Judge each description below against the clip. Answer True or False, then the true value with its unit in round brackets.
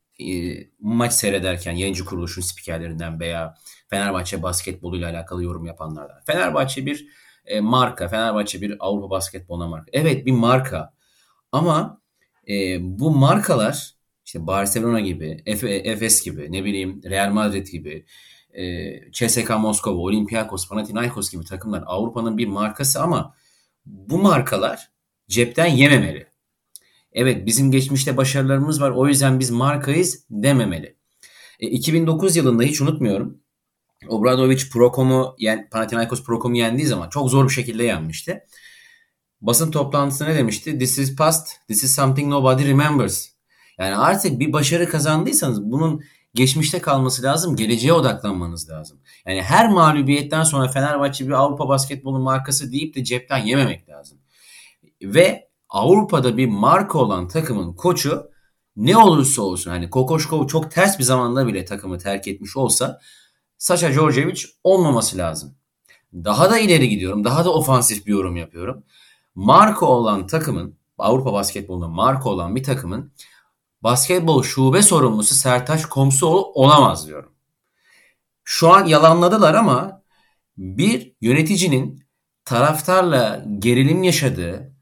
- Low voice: True (125 Hz)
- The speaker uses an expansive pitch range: True (6.4 semitones)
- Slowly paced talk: False (125 wpm)